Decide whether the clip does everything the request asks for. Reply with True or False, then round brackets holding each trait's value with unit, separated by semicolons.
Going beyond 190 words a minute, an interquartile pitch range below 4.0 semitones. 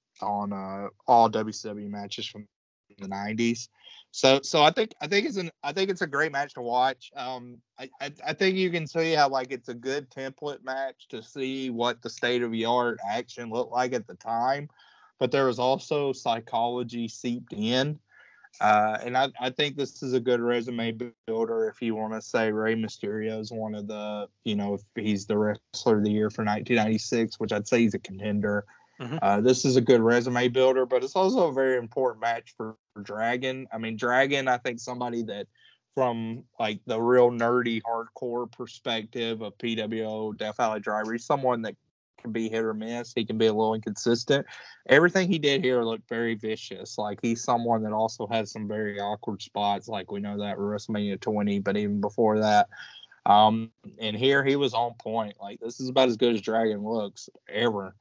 True (200 wpm; 3.1 semitones)